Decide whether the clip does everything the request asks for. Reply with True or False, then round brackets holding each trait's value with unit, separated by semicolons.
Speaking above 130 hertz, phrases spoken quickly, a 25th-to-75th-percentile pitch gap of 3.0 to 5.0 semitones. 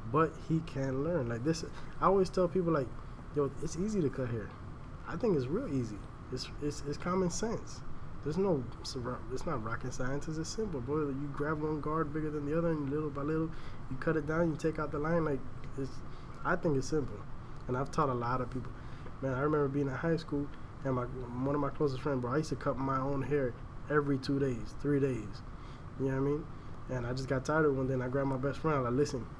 True (140 Hz; 245 wpm; 3.3 semitones)